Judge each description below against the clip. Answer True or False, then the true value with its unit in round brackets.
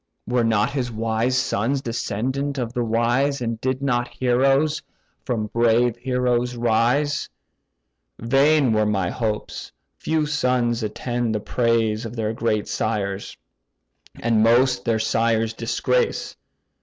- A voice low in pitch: True (120 Hz)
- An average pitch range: False (2.2 semitones)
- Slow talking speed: True (120 wpm)